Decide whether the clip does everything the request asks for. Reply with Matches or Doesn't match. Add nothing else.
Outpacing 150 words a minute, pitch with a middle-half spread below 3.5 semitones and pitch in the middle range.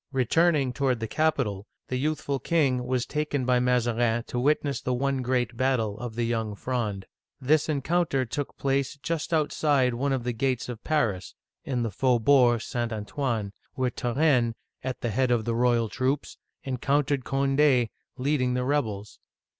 Doesn't match